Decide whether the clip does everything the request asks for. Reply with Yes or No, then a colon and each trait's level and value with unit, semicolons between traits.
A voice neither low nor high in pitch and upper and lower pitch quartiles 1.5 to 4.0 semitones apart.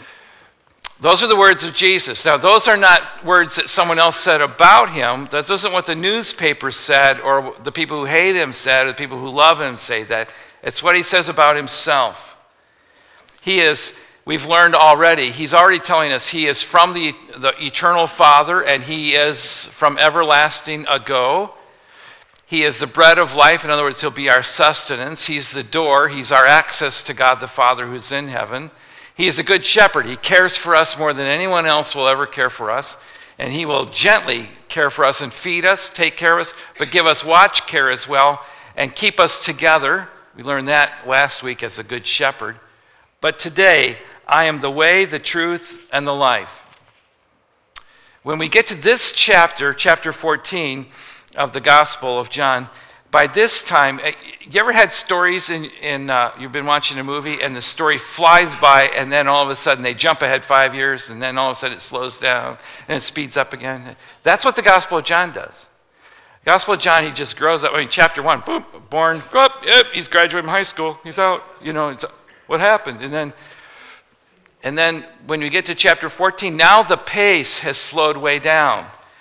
Yes: medium, 155 Hz; average, 3.7 semitones